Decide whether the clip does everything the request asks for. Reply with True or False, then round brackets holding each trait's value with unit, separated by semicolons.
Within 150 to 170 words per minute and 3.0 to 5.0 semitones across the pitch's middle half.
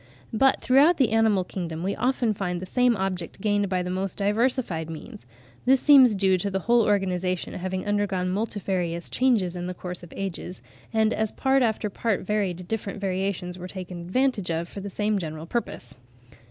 False (180 wpm; 3.5 semitones)